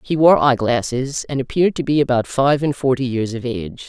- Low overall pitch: Yes, low, 130 Hz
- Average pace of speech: No, fast, 230 wpm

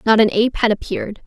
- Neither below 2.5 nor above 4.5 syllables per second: No, 7.1 syllables/s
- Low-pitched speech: No, high, 220 Hz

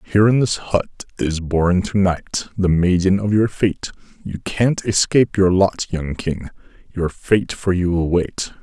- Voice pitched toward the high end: No, very low, 95 Hz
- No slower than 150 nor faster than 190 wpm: Yes, average, 180 wpm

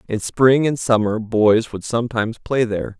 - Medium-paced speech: Yes, average, 180 wpm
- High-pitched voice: No, low, 115 Hz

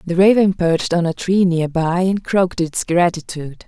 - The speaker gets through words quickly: No, average, 195 wpm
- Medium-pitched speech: Yes, medium, 175 Hz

